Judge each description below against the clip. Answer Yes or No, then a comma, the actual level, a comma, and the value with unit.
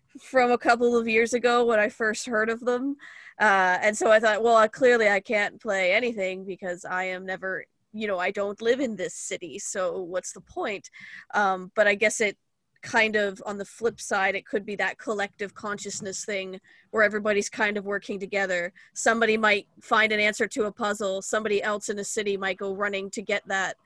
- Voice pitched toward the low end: No, high, 210 Hz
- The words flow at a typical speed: No, fast, 210 wpm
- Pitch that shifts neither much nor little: No, narrow, 2.3 semitones